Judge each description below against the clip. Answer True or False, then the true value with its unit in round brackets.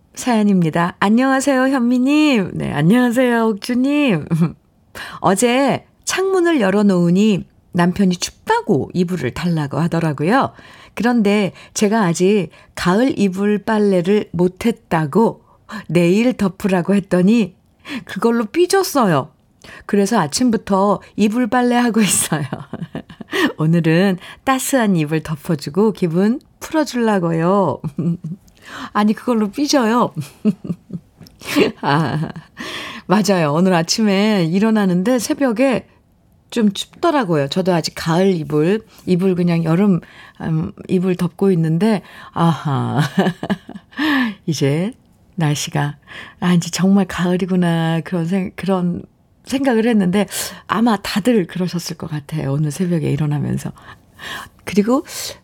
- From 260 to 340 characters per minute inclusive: False (245 characters per minute)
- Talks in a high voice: True (195 Hz)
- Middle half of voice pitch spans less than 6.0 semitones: True (5.1 semitones)